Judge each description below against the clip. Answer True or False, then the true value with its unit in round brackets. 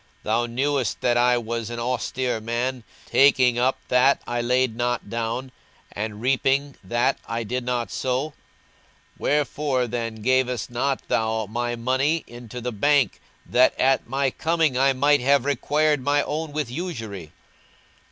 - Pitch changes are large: False (2.6 semitones)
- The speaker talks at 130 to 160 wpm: True (150 wpm)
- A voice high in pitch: False (125 Hz)